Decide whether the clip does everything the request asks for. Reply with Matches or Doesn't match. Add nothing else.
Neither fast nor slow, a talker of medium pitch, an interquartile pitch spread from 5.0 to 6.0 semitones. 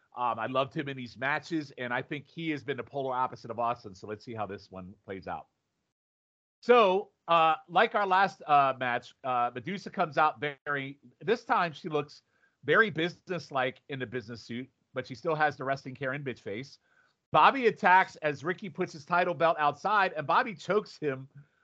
Matches